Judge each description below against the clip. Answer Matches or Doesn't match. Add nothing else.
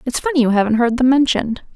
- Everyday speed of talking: Doesn't match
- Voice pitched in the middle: Doesn't match